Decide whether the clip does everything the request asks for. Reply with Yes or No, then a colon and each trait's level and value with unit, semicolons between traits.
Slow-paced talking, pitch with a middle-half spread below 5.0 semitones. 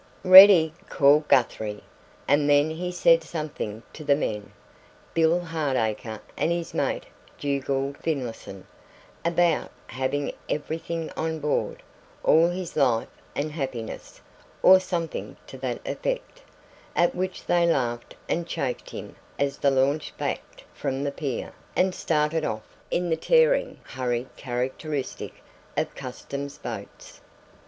Yes: slow, 125 wpm; average, 4.1 semitones